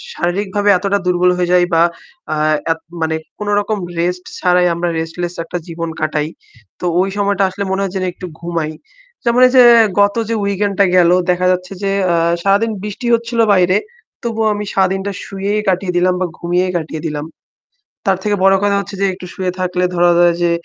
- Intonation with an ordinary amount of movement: No, narrow, 2.3 semitones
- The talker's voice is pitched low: No, medium, 185 Hz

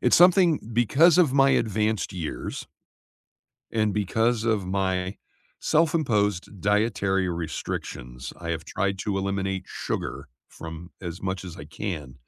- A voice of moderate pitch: No, low, 100 Hz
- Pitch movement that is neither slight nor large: Yes, average, 3.9 semitones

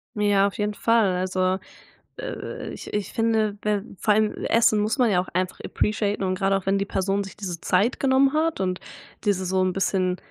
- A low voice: No, high, 200 Hz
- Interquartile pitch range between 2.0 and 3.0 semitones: Yes, narrow, 2.4 semitones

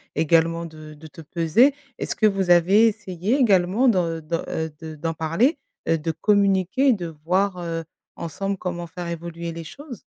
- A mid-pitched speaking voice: Yes, medium, 175 Hz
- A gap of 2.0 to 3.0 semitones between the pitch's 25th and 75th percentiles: No, average, 3.4 semitones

